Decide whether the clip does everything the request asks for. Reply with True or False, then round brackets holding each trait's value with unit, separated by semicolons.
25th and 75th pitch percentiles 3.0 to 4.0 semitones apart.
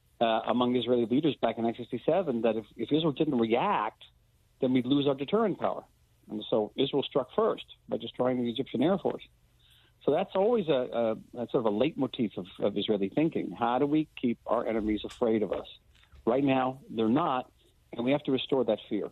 True (3.7 semitones)